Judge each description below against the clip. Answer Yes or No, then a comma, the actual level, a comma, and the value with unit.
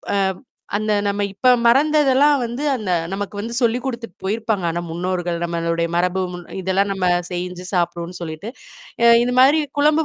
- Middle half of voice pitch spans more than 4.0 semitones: Yes, wide, 5.5 semitones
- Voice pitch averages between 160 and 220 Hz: Yes, high, 200 Hz